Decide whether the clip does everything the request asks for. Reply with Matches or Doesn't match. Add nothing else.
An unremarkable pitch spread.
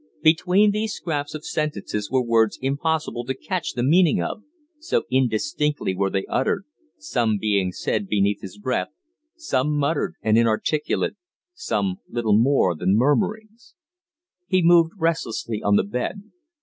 Doesn't match